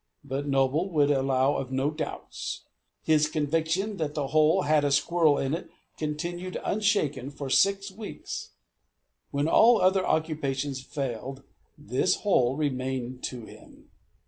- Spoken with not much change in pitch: No, average, 3.5 semitones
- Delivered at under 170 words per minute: Yes, slow, 135 wpm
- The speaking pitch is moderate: Yes, medium, 145 Hz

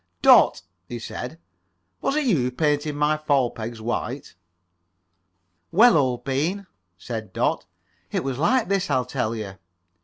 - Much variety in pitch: No, average, 4.9 semitones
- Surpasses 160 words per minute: No, average, 145 wpm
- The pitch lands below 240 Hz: Yes, low, 135 Hz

